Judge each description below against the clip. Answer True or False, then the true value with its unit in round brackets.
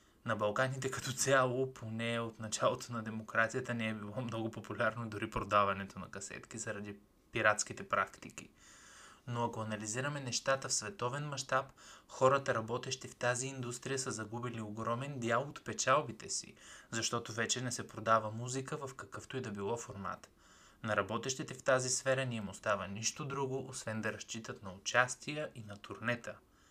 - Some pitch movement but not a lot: True (3.0 semitones)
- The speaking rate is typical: True (155 wpm)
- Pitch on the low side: True (120 Hz)